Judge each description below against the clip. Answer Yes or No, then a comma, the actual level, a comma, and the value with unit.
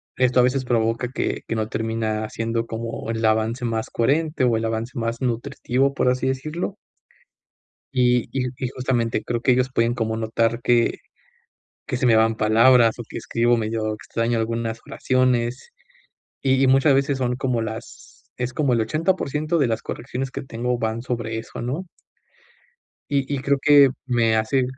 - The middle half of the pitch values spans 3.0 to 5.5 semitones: No, narrow, 2.5 semitones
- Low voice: Yes, low, 120 Hz